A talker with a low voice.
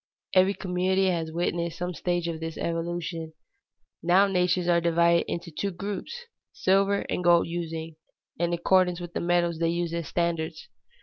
No: medium, 175 Hz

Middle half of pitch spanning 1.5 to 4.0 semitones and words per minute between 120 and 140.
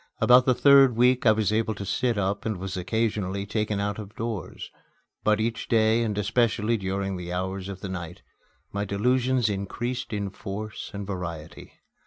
No: average, 2.9 semitones; average, 175 wpm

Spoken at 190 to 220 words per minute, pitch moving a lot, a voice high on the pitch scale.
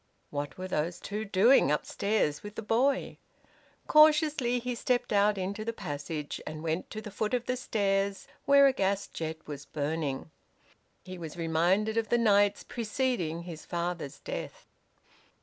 No: average, 155 wpm; wide, 5.9 semitones; high, 200 Hz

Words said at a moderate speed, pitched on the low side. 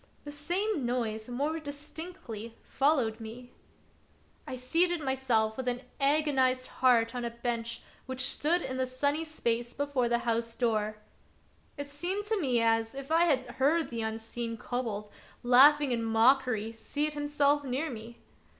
No: average, 145 wpm; very high, 255 Hz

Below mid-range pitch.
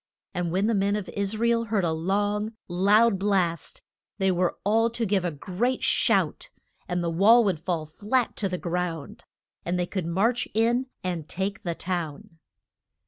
No: high, 190 Hz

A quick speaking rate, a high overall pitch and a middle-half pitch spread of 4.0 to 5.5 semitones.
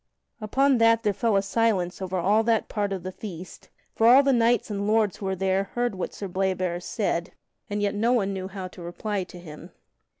No: fast, 220 wpm; high, 200 Hz; average, 3.3 semitones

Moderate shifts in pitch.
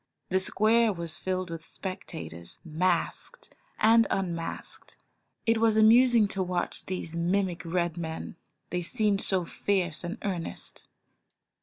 Yes: average, 3.7 semitones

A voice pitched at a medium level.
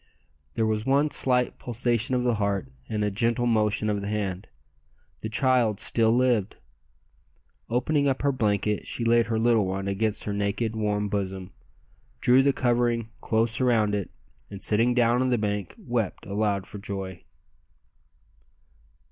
No: low, 110 Hz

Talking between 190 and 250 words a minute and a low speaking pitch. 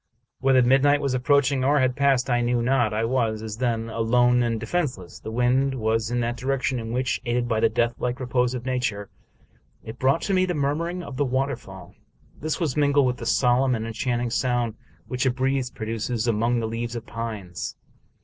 Yes: average, 200 wpm; low, 125 Hz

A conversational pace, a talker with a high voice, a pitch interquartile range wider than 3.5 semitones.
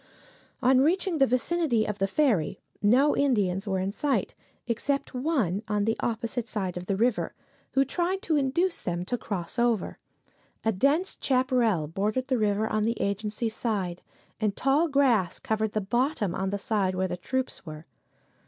Yes: average, 170 wpm; high, 225 Hz; average, 5.2 semitones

